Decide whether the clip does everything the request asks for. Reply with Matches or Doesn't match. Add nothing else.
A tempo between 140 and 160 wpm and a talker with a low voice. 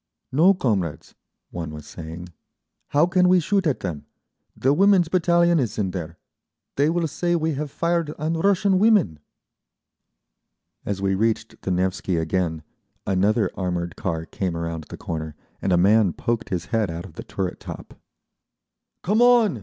Matches